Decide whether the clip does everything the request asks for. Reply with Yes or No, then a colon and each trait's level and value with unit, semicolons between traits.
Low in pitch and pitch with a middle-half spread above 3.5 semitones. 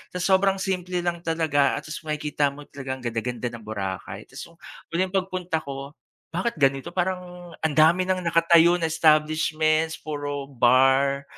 No: medium, 155 Hz; average, 4.1 semitones